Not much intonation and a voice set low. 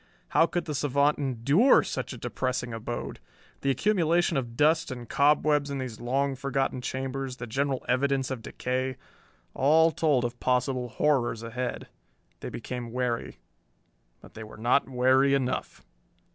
Yes: narrow, 2.3 semitones; low, 130 Hz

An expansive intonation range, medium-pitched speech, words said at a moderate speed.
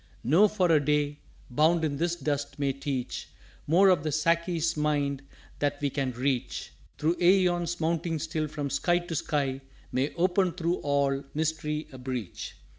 No: average, 3.2 semitones; medium, 150 Hz; average, 165 wpm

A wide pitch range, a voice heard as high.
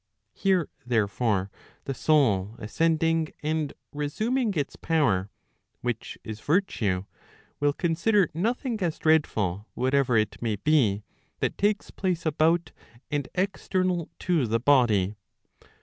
No: wide, 7.5 semitones; medium, 145 Hz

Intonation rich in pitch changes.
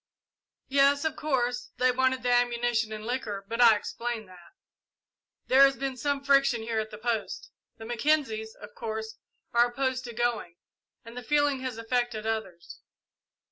No: average, 3.0 semitones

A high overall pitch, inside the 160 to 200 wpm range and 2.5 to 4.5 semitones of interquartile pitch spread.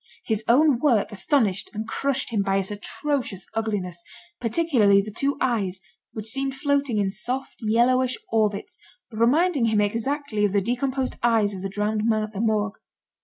Yes: high, 225 Hz; average, 165 wpm; average, 4.0 semitones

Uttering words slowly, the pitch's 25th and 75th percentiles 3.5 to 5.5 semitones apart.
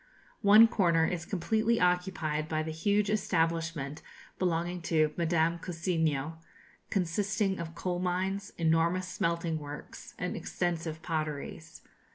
No: slow, 115 wpm; narrow, 2.5 semitones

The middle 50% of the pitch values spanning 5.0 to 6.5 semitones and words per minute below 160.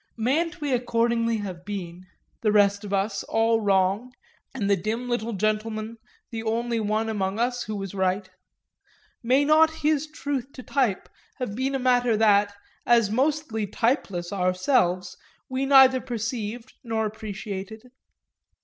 No: average, 3.8 semitones; average, 140 wpm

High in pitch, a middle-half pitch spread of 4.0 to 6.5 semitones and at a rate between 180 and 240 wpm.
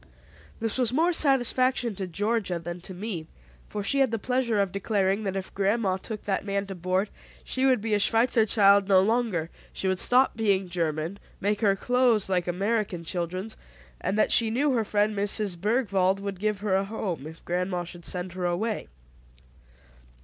No: high, 200 Hz; average, 3.4 semitones; average, 185 wpm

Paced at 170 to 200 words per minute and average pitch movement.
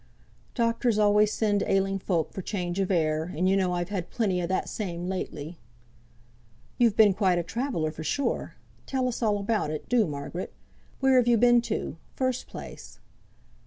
Yes: average, 175 wpm; average, 4.8 semitones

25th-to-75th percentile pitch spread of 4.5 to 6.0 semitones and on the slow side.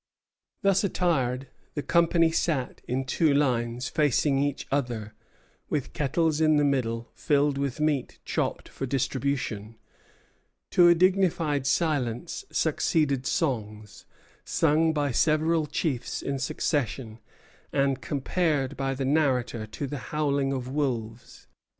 No: average, 3.5 semitones; slow, 120 wpm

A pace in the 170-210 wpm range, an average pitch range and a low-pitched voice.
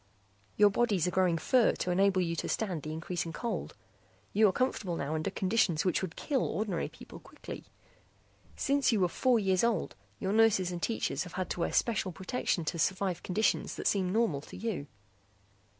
No: average, 185 wpm; average, 4.0 semitones; high, 190 Hz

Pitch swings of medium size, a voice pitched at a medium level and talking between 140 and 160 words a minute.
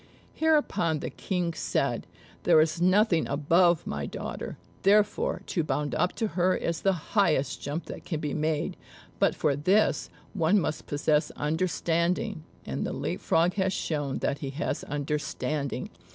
Yes: average, 3.8 semitones; medium, 165 Hz; average, 150 wpm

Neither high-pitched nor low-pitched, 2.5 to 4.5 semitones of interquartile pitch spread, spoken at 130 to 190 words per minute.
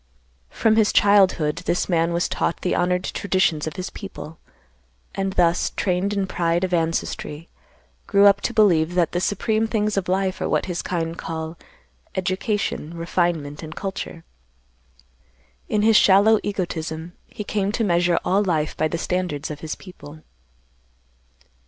Yes: medium, 180 Hz; average, 3.3 semitones; average, 150 wpm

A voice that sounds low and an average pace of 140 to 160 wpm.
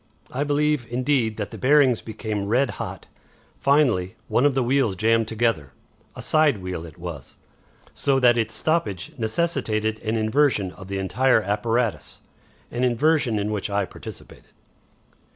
Yes: low, 115 Hz; average, 150 wpm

